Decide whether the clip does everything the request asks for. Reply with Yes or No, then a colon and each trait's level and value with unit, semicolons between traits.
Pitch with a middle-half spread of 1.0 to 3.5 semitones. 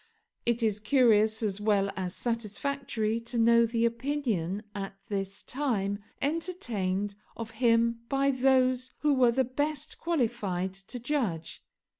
No: average, 4.2 semitones